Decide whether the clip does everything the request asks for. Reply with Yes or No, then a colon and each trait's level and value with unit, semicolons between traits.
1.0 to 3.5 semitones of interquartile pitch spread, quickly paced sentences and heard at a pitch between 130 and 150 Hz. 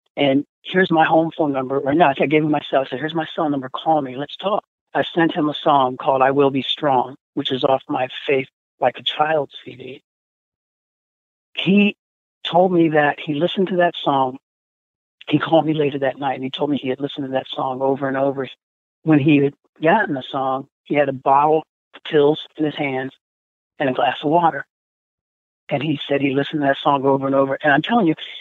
Yes: average, 2.7 semitones; fast, 220 wpm; medium, 140 Hz